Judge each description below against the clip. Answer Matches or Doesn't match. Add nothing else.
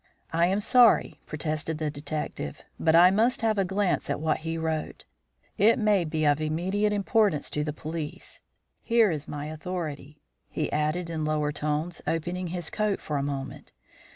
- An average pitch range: Matches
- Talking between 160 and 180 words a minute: Matches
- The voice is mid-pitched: Matches